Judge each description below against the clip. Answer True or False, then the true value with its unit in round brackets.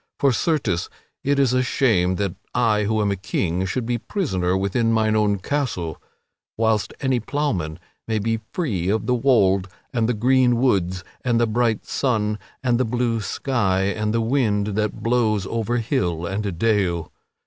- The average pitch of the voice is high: False (110 Hz)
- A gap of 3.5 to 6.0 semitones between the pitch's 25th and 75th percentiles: True (4.0 semitones)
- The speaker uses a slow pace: False (170 wpm)